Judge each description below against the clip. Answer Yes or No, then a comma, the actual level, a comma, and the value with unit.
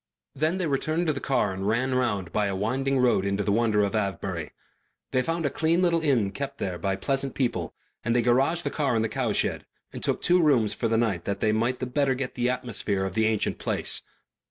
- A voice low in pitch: Yes, low, 120 Hz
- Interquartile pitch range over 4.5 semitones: Yes, average, 5.2 semitones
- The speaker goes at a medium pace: No, fast, 230 wpm